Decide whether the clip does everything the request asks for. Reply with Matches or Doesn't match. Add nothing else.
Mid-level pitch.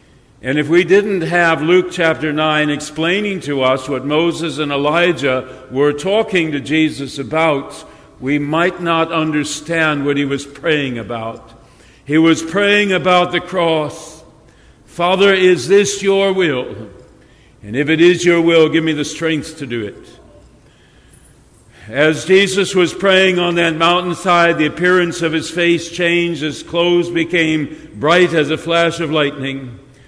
Matches